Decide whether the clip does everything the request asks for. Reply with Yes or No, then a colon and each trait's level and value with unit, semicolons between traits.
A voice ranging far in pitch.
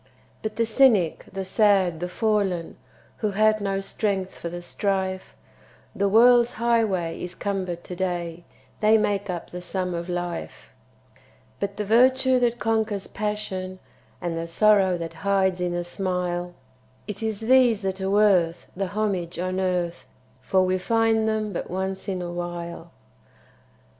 No: average, 3.2 semitones